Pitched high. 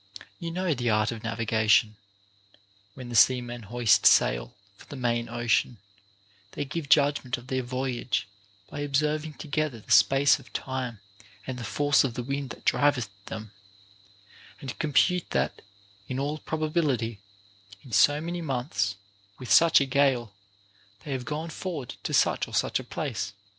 No: low, 130 Hz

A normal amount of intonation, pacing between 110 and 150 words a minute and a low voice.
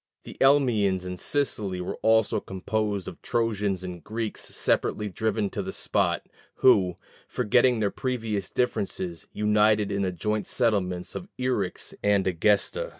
Yes: average, 3.2 semitones; average, 140 wpm; low, 105 Hz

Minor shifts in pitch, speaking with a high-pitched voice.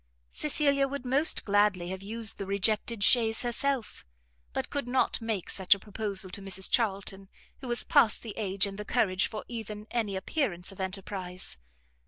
No: average, 3.7 semitones; high, 210 Hz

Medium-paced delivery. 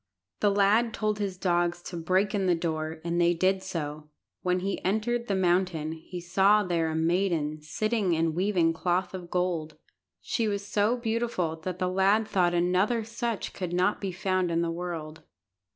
Yes: average, 180 wpm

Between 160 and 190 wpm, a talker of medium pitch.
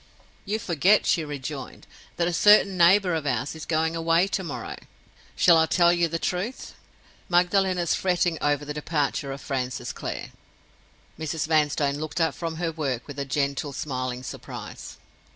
Yes: average, 165 wpm; medium, 160 Hz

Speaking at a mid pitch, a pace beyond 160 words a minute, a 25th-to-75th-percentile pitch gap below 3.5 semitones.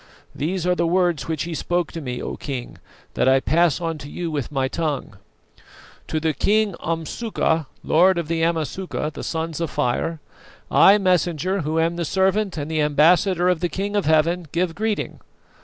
Yes: medium, 165 Hz; average, 185 wpm; average, 2.7 semitones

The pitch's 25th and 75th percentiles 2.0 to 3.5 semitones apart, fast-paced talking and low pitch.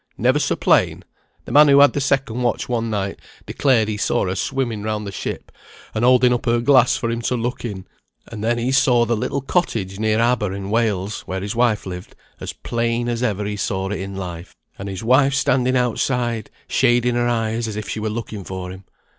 Yes: average, 3.2 semitones; fast, 215 wpm; low, 115 Hz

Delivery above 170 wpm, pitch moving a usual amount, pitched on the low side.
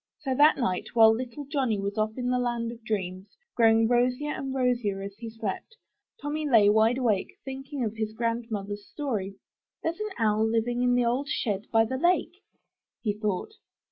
No: average, 185 wpm; average, 3.4 semitones; high, 230 Hz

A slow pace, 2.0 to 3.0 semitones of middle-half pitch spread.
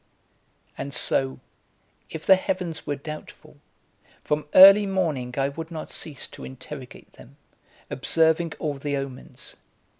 No: slow, 125 wpm; average, 3.4 semitones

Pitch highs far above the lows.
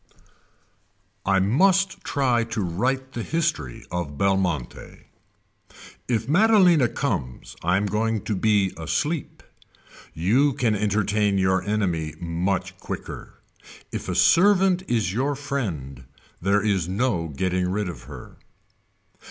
Yes: wide, 6.6 semitones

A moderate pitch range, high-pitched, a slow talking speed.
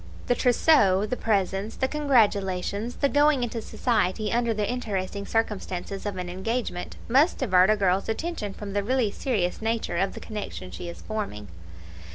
No: average, 4.1 semitones; high, 210 Hz; average, 165 wpm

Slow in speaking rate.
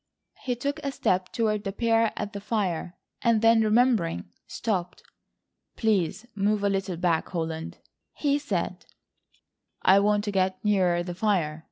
No: average, 150 wpm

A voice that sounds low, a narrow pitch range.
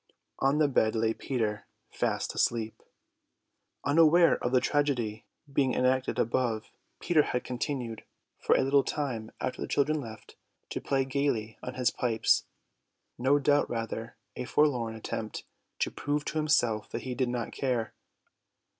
No: low, 125 Hz; average, 3.9 semitones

